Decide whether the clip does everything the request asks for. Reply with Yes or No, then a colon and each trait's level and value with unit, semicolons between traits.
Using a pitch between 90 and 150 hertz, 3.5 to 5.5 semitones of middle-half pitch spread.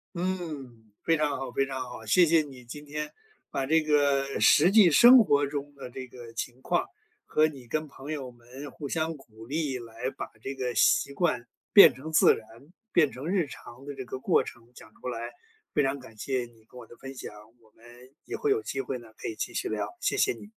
Yes: low, 135 Hz; average, 4.0 semitones